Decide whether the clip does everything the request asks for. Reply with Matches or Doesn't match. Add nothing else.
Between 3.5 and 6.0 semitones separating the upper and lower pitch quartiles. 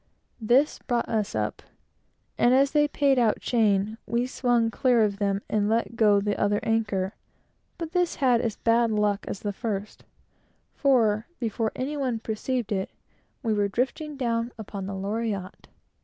Doesn't match